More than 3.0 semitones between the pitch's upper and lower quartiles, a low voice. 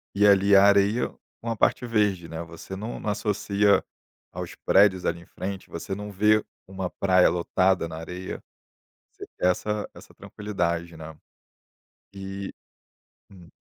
No: narrow, 2.6 semitones; very low, 95 Hz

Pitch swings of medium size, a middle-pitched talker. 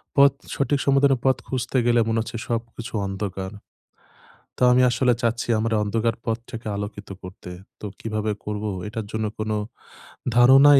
No: average, 3.0 semitones; low, 115 Hz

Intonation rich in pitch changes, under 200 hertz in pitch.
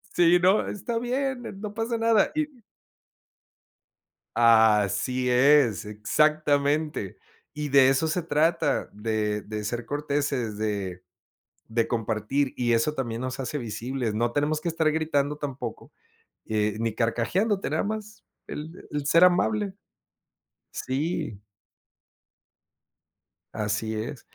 Yes: wide, 6.4 semitones; medium, 140 Hz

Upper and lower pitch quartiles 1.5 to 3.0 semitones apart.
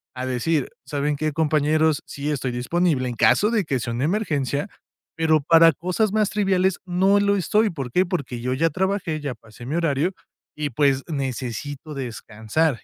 No: average, 5.1 semitones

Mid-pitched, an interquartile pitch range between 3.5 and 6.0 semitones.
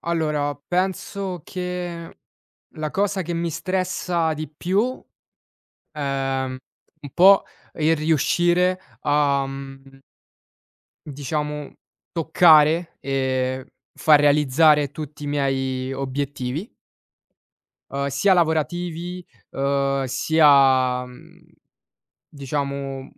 Yes: medium, 150 Hz; average, 3.9 semitones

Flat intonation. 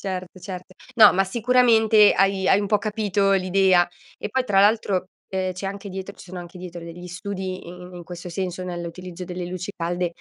Yes: narrow, 2.0 semitones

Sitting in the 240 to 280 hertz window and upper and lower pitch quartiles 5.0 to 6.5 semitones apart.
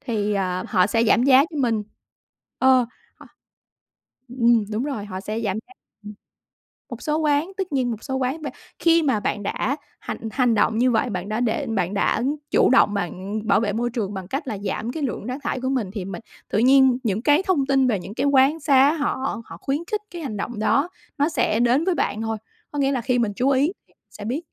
No: high, 245 Hz; average, 4.6 semitones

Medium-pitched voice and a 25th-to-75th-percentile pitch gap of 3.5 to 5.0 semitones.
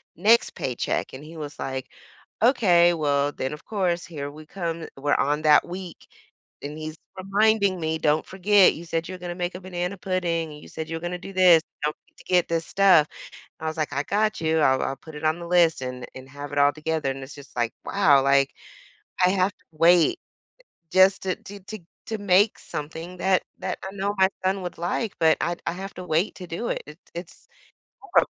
Yes: medium, 170 Hz; average, 3.8 semitones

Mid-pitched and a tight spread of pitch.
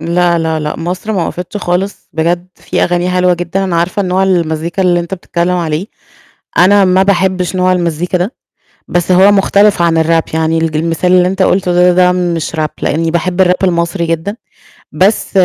Yes: medium, 180 Hz; narrow, 1.7 semitones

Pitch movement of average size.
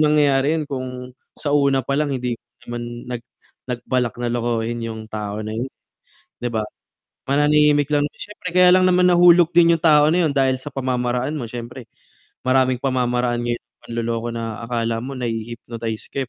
Yes: average, 3.8 semitones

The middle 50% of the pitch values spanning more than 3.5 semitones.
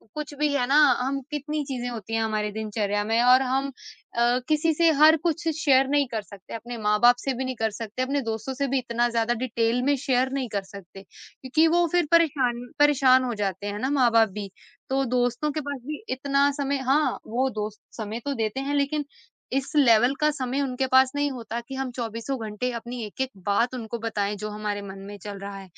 Yes: average, 4.0 semitones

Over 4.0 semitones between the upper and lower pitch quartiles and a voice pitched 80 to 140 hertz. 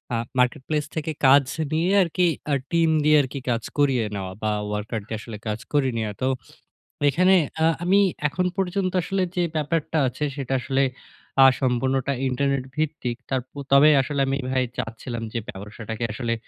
Yes: average, 4.8 semitones; low, 135 Hz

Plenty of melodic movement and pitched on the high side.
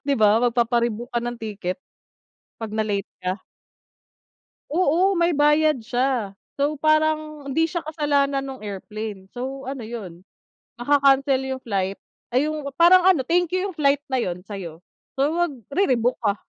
Yes: wide, 5.8 semitones; very high, 265 Hz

